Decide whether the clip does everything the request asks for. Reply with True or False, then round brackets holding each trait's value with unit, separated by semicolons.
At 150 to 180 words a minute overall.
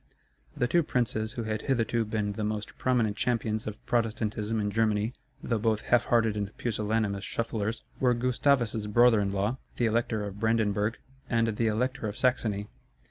True (165 wpm)